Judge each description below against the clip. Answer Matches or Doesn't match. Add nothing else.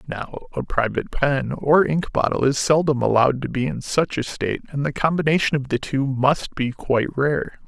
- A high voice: Doesn't match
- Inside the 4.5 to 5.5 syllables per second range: Matches